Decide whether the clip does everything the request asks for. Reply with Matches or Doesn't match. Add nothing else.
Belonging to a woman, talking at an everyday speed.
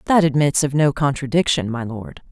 Matches